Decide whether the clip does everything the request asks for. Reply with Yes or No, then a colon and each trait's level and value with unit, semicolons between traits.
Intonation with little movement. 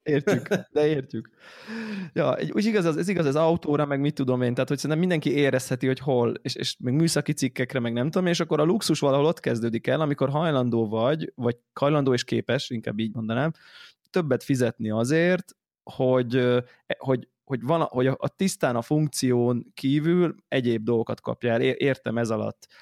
No: average, 4.4 semitones